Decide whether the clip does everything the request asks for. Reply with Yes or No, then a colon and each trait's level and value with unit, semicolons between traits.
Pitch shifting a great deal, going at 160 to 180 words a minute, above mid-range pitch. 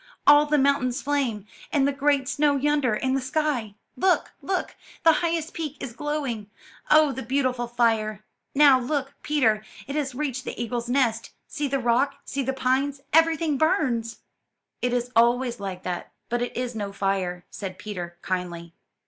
No: average, 4.2 semitones; average, 165 wpm; very high, 255 Hz